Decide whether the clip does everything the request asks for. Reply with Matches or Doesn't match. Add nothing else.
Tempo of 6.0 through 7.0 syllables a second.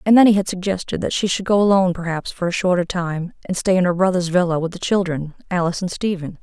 Matches